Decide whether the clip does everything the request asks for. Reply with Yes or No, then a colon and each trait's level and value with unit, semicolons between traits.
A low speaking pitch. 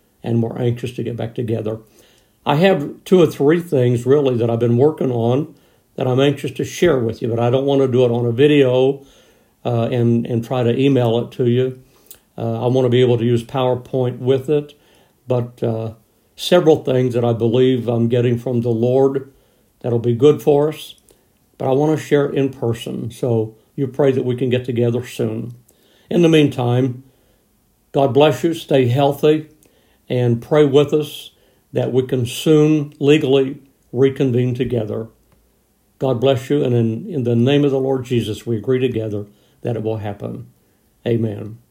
Yes: low, 125 Hz